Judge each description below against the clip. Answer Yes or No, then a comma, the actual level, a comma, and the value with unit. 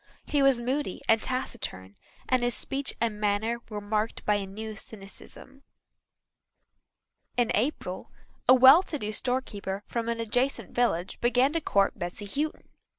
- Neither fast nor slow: Yes, average, 150 wpm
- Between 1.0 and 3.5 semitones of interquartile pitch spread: No, average, 4.0 semitones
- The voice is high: Yes, high, 230 Hz